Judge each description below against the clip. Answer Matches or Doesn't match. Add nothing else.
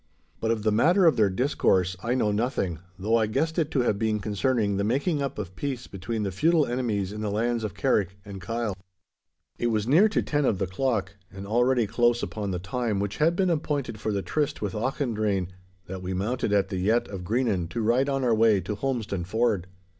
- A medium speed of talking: Doesn't match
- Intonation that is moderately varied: Matches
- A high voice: Doesn't match